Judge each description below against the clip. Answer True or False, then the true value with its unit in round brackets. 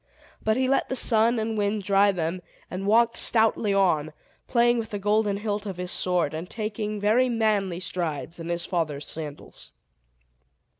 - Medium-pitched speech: False (205 Hz)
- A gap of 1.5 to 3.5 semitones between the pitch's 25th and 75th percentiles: False (3.9 semitones)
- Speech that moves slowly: False (165 wpm)